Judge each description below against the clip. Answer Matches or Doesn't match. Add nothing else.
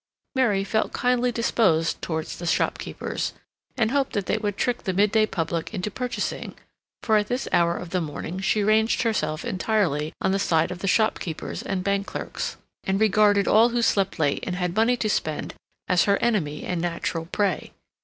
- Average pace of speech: Matches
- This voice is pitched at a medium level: Doesn't match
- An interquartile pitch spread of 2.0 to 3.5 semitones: Doesn't match